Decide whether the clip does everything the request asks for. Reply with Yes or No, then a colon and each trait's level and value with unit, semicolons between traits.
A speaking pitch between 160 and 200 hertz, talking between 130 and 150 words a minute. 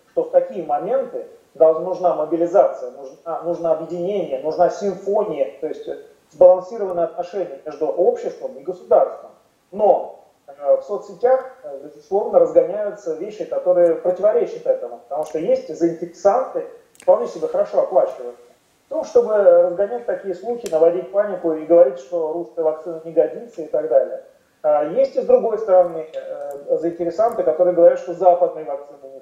Yes: high, 190 Hz; average, 140 wpm